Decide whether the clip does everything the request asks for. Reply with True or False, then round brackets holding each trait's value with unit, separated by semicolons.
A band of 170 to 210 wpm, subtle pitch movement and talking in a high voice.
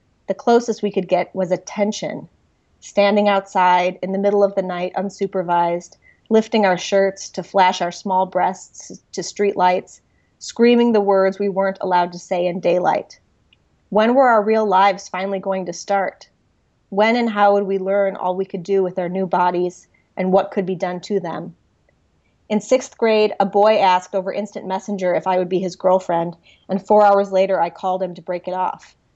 True (190 wpm; 1.8 semitones; 195 Hz)